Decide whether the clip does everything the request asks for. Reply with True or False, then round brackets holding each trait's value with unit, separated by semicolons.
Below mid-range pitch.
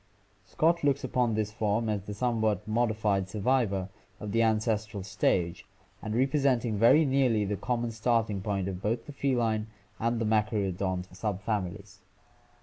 True (110 Hz)